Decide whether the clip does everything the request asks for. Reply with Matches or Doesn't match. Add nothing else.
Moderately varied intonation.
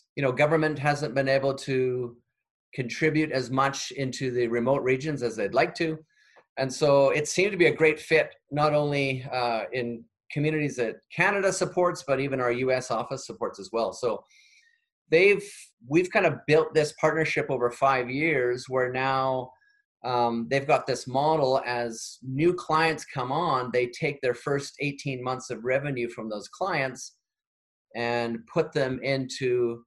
Matches